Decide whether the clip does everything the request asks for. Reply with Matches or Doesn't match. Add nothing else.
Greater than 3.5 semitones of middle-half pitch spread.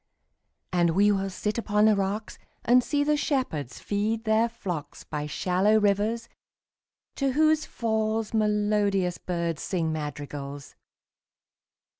Matches